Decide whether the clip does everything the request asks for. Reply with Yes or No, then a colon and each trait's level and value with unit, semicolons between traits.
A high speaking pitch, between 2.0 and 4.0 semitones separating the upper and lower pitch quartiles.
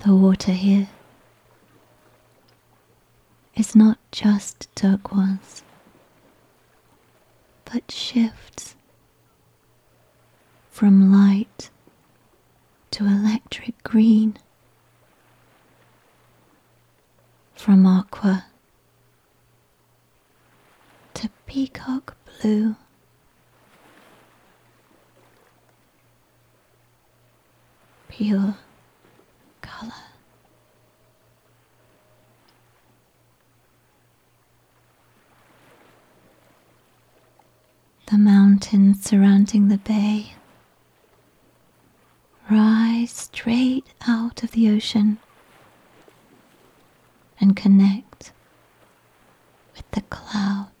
Yes: high, 205 Hz; narrow, 2.4 semitones